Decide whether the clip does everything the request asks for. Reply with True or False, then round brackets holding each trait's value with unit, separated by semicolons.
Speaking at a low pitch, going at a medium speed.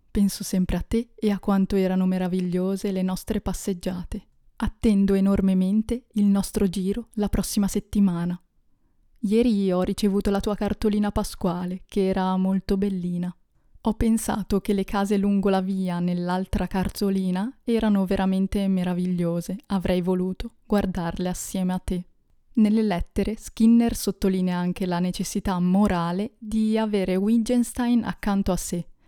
False (195 Hz; 135 wpm)